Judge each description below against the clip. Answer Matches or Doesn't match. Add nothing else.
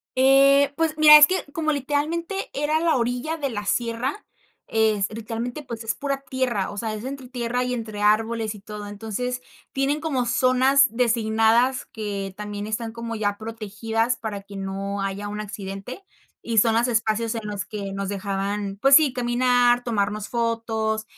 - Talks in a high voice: Matches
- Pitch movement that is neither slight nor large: Matches